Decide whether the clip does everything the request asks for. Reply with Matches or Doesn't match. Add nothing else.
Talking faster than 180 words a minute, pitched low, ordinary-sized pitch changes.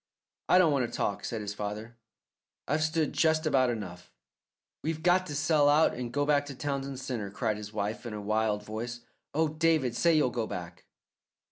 Doesn't match